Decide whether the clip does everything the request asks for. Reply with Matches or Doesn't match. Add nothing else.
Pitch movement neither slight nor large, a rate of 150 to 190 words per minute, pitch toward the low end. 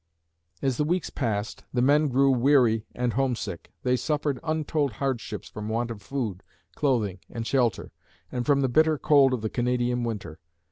Matches